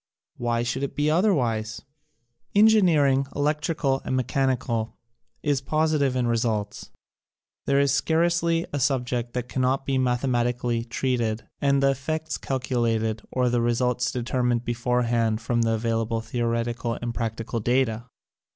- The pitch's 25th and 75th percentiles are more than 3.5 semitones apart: No, average, 2.8 semitones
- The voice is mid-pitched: No, low, 125 Hz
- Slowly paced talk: Yes, slow, 130 wpm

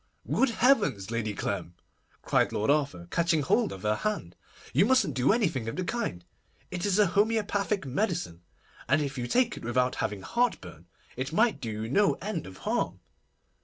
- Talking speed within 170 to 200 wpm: Yes, average, 175 wpm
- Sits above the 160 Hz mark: No, medium, 150 Hz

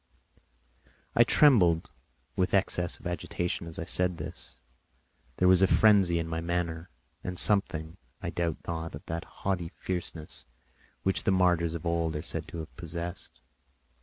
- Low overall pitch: Yes, very low, 85 Hz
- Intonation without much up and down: Yes, narrow, 1.9 semitones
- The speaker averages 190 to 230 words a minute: No, average, 155 wpm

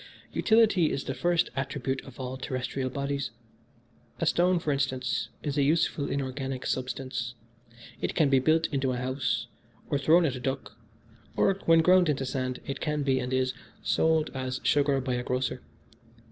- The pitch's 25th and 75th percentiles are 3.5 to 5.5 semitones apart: No, average, 2.7 semitones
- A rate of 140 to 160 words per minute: No, average, 170 wpm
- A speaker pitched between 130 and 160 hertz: Yes, low, 135 Hz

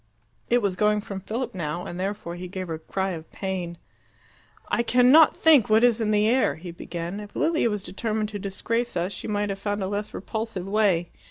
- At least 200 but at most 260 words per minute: Yes, fast, 205 wpm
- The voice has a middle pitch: No, high, 205 Hz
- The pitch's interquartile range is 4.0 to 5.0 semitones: No, average, 3.2 semitones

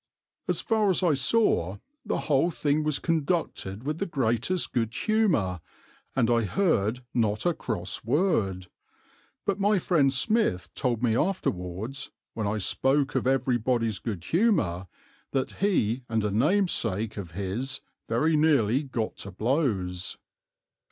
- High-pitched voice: No, low, 125 Hz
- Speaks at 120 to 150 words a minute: Yes, average, 140 wpm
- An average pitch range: No, wide, 7.3 semitones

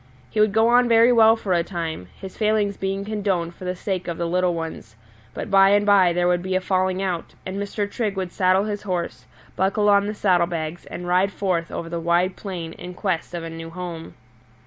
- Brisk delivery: Yes, fast, 225 wpm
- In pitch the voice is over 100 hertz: Yes, medium, 185 Hz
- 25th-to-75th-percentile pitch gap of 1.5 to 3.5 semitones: Yes, average, 2.8 semitones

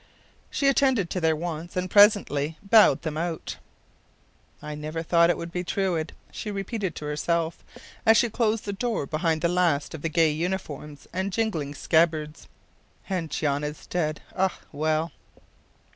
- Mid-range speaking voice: Yes, medium, 170 Hz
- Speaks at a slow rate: No, average, 160 wpm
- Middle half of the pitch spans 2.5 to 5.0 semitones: Yes, average, 3.7 semitones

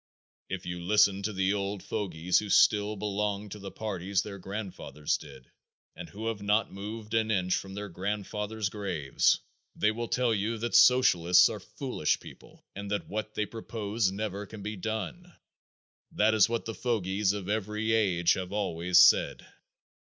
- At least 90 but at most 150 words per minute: No, average, 170 wpm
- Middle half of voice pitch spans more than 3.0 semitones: No, narrow, 2.4 semitones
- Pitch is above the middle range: No, low, 105 Hz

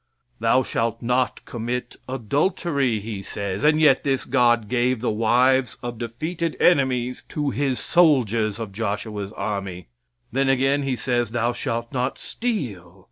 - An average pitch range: Yes, average, 3.4 semitones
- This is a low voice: Yes, low, 120 Hz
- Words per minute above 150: No, average, 140 wpm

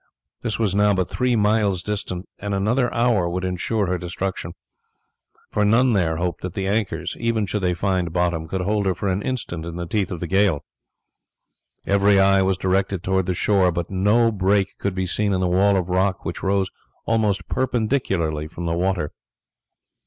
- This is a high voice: No, very low, 95 Hz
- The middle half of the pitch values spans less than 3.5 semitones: Yes, narrow, 2.6 semitones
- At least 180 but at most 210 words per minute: Yes, average, 190 wpm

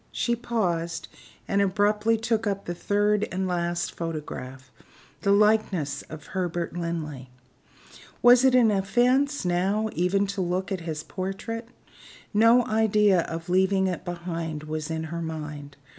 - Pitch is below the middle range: No, medium, 185 Hz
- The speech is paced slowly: No, average, 145 wpm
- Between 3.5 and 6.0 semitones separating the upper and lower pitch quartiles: Yes, average, 4.2 semitones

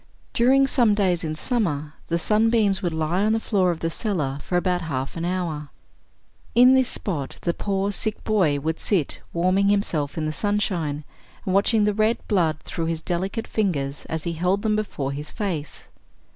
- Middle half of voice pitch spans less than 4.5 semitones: No, average, 4.8 semitones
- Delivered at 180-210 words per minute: Yes, average, 185 wpm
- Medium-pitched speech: Yes, medium, 180 Hz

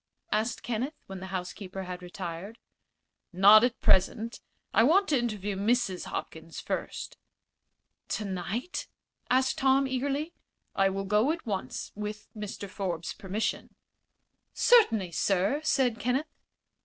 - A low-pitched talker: No, high, 210 Hz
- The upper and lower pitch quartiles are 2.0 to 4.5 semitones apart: No, average, 5.0 semitones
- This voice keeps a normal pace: No, slow, 120 wpm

